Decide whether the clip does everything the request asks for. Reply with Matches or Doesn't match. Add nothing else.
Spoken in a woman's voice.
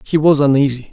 Doesn't match